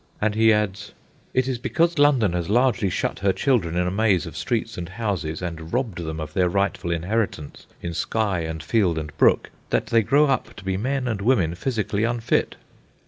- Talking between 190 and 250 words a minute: Yes, average, 195 wpm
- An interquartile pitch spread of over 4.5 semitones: Yes, average, 5.2 semitones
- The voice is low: Yes, low, 100 Hz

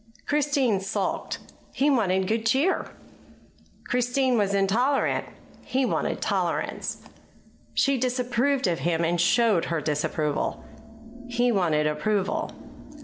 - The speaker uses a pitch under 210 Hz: No, high, 225 Hz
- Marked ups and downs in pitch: Yes, wide, 6.3 semitones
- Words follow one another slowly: Yes, slow, 105 wpm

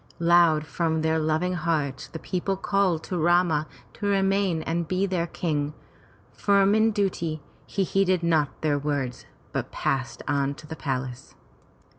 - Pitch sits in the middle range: Yes, medium, 165 Hz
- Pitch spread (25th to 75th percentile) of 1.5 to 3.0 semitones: No, average, 3.5 semitones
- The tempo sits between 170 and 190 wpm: No, average, 150 wpm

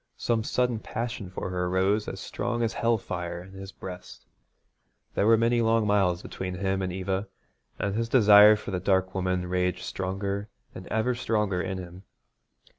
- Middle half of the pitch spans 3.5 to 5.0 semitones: No, average, 3.1 semitones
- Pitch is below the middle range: Yes, very low, 95 Hz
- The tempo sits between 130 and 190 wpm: Yes, average, 175 wpm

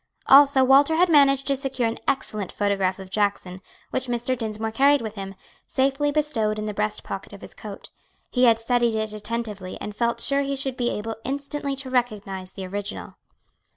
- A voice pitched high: Yes, high, 235 Hz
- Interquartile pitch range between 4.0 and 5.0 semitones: Yes, average, 4.6 semitones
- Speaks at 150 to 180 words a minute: No, average, 190 wpm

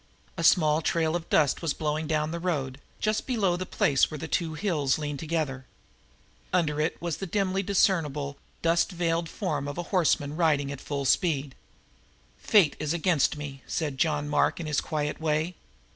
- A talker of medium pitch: Yes, medium, 155 Hz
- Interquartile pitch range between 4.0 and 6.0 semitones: No, average, 2.7 semitones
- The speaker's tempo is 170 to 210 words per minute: Yes, average, 175 wpm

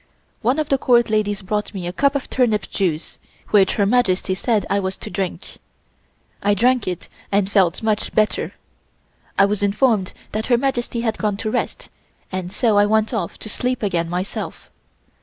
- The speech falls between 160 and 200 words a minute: Yes, average, 180 wpm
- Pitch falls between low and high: No, high, 210 Hz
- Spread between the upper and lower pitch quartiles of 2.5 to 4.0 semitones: Yes, average, 3.5 semitones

